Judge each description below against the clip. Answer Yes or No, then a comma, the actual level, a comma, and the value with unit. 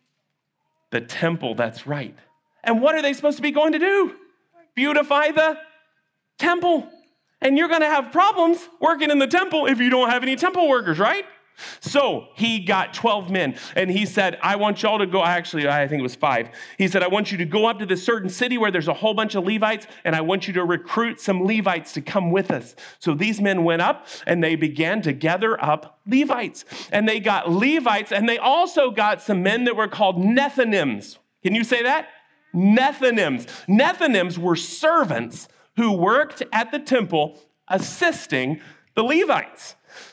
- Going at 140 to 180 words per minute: No, average, 190 wpm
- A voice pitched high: Yes, high, 220 Hz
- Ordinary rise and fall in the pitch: No, wide, 7.7 semitones